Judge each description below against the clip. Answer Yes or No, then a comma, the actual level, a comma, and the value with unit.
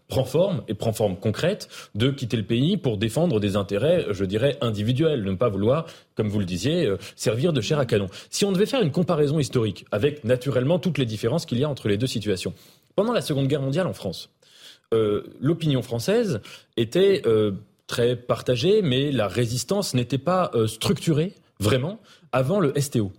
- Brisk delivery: No, average, 195 wpm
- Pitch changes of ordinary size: No, wide, 6.4 semitones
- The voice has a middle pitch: No, low, 125 Hz